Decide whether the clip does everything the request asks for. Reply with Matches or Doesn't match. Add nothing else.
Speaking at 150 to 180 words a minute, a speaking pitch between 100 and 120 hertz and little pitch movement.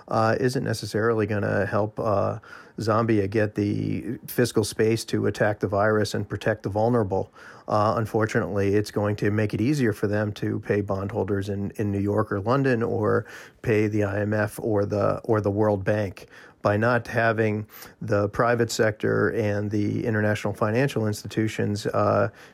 Matches